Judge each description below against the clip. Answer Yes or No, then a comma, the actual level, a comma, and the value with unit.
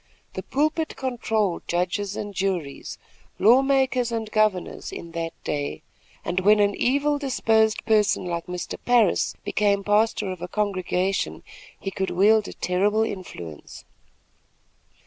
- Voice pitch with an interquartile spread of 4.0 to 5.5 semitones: No, average, 3.6 semitones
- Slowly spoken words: Yes, slow, 130 wpm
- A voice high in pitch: Yes, high, 205 Hz